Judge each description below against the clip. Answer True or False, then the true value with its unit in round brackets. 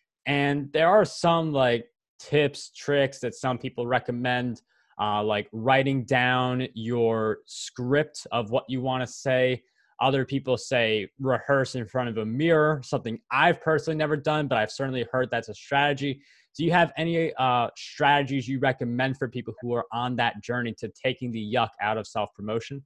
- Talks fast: False (175 wpm)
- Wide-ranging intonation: False (3.0 semitones)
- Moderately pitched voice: False (130 Hz)